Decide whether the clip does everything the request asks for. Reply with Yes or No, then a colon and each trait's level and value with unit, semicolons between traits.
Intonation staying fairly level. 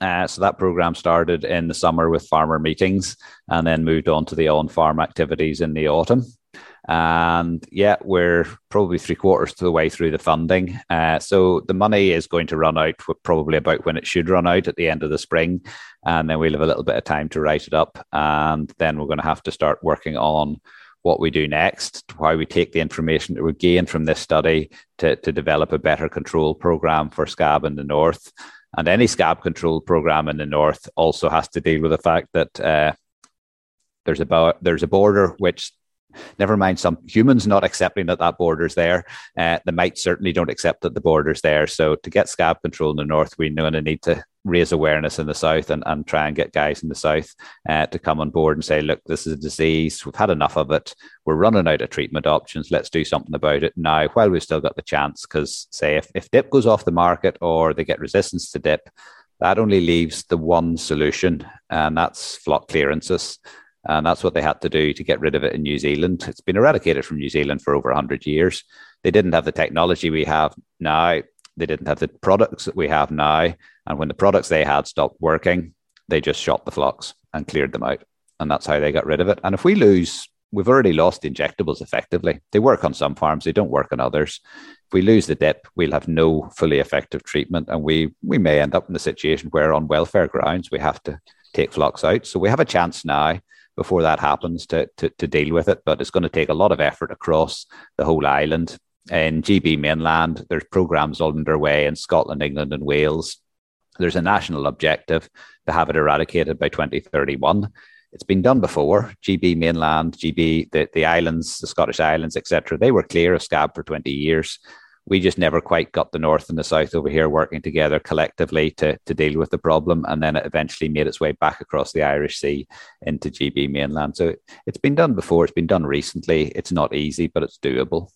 Yes: narrow, 1.8 semitones